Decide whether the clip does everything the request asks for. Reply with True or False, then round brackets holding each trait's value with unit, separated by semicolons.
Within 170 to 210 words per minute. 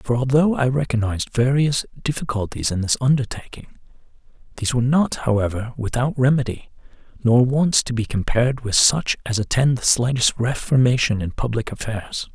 False (145 wpm)